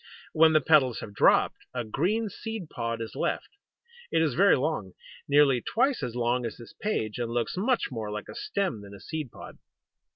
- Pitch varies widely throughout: Yes, wide, 7.5 semitones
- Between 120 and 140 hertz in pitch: Yes, low, 135 Hz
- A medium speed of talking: Yes, average, 195 wpm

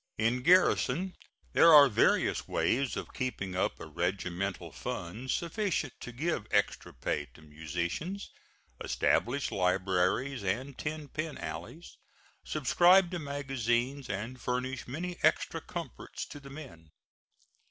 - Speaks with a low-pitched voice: Yes, low, 130 Hz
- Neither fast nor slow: No, slow, 120 wpm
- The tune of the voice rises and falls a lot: Yes, wide, 7.7 semitones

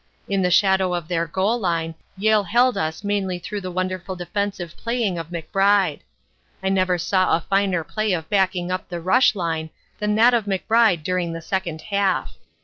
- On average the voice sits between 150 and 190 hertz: Yes, medium, 185 Hz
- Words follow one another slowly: No, average, 180 wpm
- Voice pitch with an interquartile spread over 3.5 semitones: No, average, 2.7 semitones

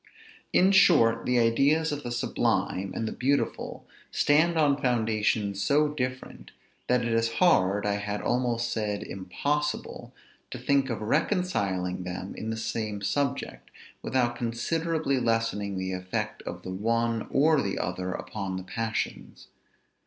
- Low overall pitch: Yes, low, 115 Hz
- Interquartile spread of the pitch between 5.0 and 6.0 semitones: Yes, wide, 5.5 semitones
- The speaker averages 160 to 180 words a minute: No, average, 140 wpm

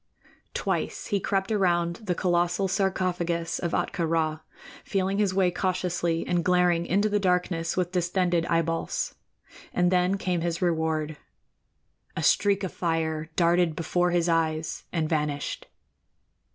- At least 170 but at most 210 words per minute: No, slow, 135 wpm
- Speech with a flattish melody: Yes, narrow, 1.9 semitones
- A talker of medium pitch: Yes, medium, 175 Hz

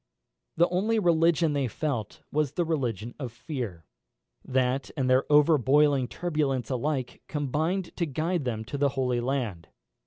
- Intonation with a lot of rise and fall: No, average, 4.0 semitones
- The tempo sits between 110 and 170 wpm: Yes, average, 145 wpm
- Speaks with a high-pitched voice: No, medium, 140 Hz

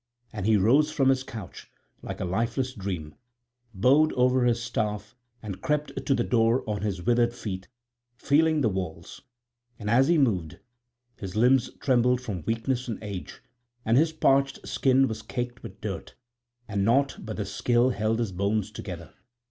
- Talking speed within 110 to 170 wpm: Yes, average, 165 wpm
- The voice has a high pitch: No, low, 115 Hz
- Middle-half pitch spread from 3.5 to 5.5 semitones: Yes, average, 4.3 semitones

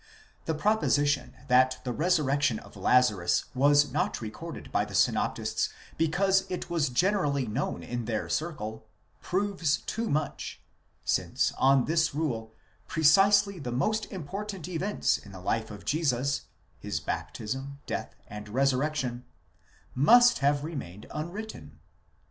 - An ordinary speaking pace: No, slow, 125 wpm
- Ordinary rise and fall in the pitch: No, wide, 5.9 semitones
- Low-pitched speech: No, medium, 145 Hz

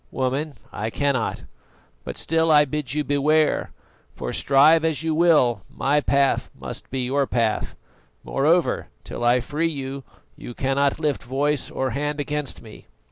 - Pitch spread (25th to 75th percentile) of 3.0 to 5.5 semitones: No, narrow, 2.4 semitones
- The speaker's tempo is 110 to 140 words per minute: No, average, 150 wpm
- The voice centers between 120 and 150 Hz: Yes, medium, 140 Hz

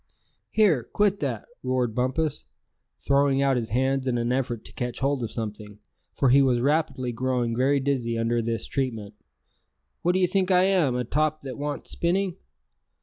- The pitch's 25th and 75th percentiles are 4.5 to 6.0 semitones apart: No, average, 3.7 semitones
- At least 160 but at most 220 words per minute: Yes, average, 170 wpm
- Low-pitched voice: Yes, low, 130 Hz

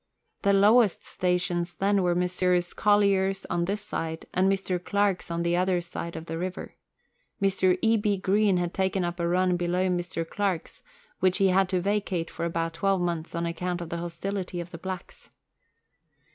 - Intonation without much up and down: Yes, narrow, 2.1 semitones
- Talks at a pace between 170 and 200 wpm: Yes, average, 180 wpm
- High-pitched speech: No, medium, 180 Hz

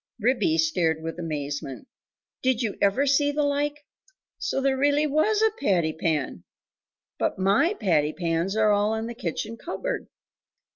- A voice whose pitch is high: Yes, high, 215 Hz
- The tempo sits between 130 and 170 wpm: Yes, average, 150 wpm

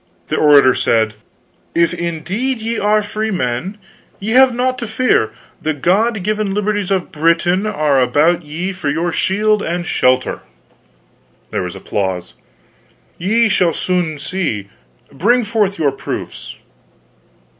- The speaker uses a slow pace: Yes, slow, 125 wpm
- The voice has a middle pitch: Yes, medium, 180 Hz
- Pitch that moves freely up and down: Yes, wide, 6.2 semitones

